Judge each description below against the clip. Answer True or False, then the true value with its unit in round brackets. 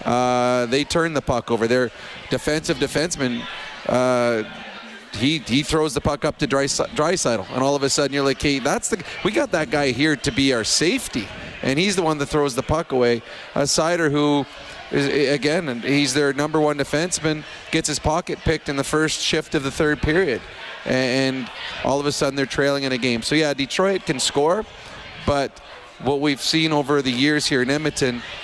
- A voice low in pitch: False (145 Hz)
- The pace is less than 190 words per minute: False (200 wpm)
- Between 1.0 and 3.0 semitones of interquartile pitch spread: True (2.4 semitones)